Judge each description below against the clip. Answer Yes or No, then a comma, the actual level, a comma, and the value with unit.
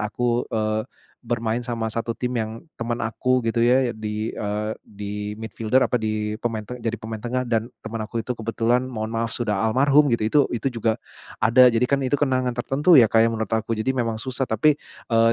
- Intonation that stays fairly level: Yes, narrow, 2.2 semitones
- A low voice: Yes, low, 115 Hz